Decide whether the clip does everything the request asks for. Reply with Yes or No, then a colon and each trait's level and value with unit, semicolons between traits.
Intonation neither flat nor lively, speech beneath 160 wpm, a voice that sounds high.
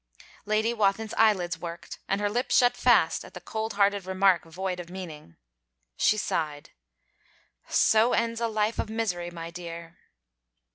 Yes: average, 4.1 semitones; average, 150 wpm; high, 195 Hz